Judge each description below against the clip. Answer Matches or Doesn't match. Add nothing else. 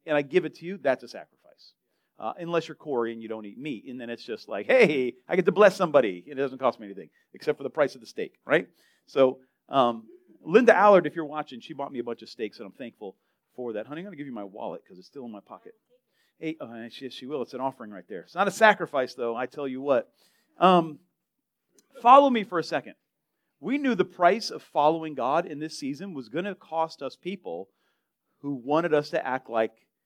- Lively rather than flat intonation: Matches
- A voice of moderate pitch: Matches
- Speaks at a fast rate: Matches